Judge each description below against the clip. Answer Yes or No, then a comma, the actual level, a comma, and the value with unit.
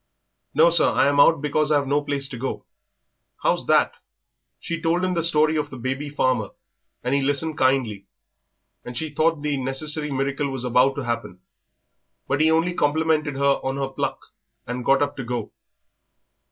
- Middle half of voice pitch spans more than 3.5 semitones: No, narrow, 2.6 semitones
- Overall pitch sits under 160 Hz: Yes, medium, 140 Hz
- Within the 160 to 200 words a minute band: Yes, average, 175 wpm